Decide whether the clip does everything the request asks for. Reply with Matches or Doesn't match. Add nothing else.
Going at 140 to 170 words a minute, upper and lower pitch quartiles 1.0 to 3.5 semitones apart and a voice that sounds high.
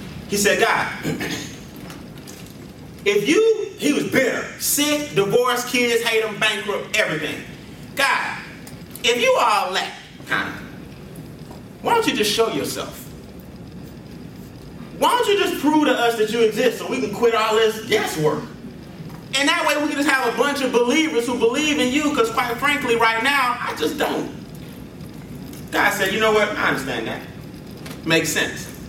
Doesn't match